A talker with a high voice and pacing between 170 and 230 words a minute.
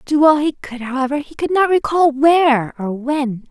Yes: very high, 280 Hz; fast, 205 wpm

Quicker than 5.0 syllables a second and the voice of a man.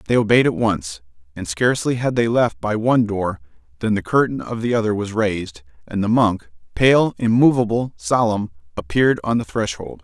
Yes: 5.2 syllables/s; male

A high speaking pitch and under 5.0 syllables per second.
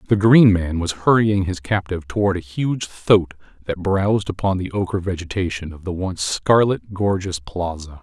No: very low, 95 Hz; 4.7 syllables/s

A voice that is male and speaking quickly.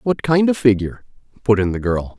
Yes: male; fast, 220 wpm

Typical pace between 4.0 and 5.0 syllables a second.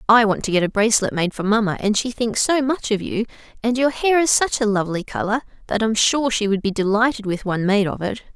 No: 6.2 syllables/s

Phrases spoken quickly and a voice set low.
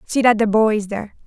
No: fast, 285 wpm; high, 215 Hz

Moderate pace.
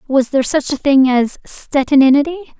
Yes: average, 160 wpm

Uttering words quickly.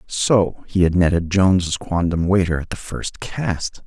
No: average, 170 wpm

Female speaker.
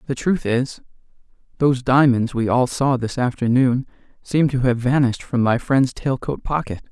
No: male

